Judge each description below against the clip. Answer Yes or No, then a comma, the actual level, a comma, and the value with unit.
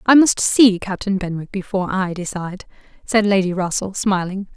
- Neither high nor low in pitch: No, high, 195 Hz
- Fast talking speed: No, average, 160 wpm